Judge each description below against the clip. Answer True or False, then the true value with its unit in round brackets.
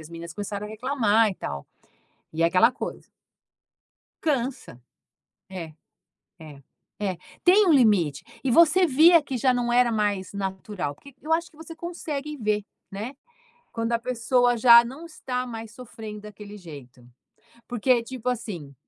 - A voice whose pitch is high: True (230 Hz)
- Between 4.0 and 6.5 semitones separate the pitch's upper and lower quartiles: True (5.0 semitones)